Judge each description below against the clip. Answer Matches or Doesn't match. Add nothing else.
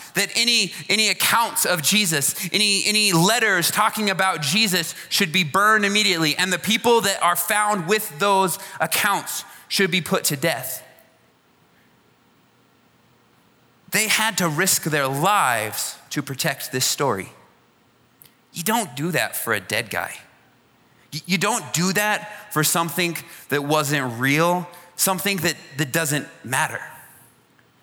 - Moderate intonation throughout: Matches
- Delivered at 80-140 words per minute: Matches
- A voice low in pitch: Doesn't match